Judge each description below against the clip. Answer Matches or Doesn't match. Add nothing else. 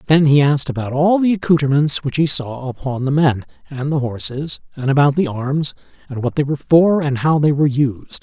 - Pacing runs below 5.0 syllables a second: Doesn't match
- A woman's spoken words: Doesn't match